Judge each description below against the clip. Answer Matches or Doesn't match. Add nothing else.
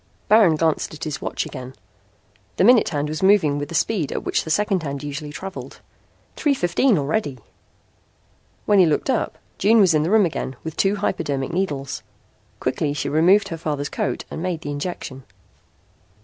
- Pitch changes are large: Doesn't match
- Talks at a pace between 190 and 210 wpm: Doesn't match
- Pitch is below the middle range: Doesn't match